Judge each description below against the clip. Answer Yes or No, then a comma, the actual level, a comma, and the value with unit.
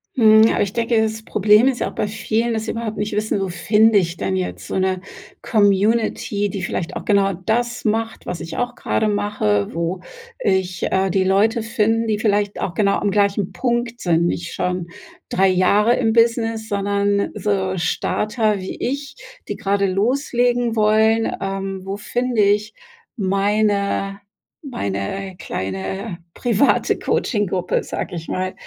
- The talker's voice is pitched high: Yes, high, 205 Hz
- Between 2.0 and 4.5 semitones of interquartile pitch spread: Yes, average, 2.9 semitones